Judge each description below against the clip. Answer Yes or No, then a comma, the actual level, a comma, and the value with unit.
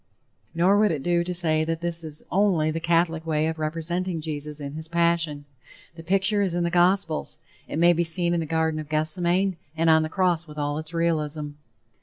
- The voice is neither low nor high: Yes, medium, 165 Hz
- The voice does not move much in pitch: Yes, narrow, 1.8 semitones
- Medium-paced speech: No, fast, 210 wpm